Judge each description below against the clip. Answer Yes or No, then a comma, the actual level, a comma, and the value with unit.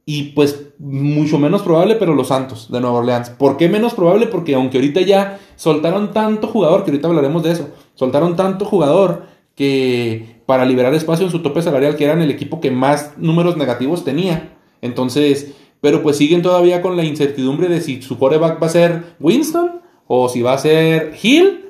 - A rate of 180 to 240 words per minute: Yes, fast, 190 wpm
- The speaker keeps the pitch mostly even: No, average, 4.4 semitones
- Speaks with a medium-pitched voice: Yes, medium, 155 Hz